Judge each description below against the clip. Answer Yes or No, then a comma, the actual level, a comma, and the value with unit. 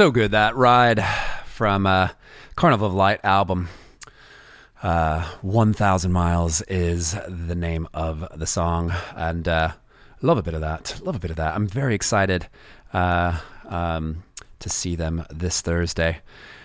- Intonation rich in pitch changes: No, average, 3.4 semitones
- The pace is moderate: Yes, average, 150 wpm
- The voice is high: No, very low, 90 Hz